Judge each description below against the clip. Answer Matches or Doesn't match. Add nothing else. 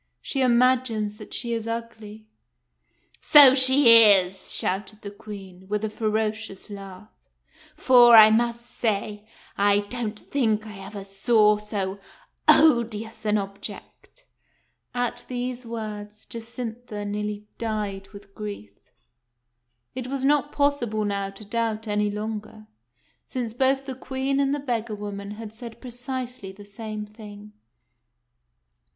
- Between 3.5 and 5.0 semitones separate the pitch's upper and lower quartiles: Doesn't match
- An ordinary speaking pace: Doesn't match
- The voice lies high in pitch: Matches